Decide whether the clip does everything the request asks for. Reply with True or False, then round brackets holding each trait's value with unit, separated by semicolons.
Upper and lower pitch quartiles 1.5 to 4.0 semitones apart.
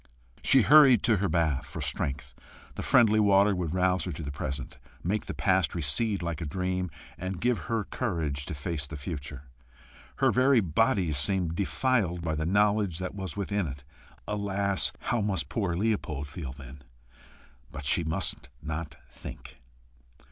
False (5.2 semitones)